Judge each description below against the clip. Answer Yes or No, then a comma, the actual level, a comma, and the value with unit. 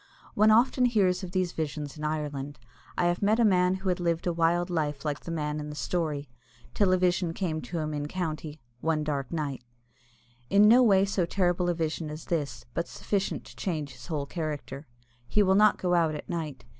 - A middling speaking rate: No, fast, 210 wpm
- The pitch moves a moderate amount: Yes, average, 3.5 semitones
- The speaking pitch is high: No, medium, 170 Hz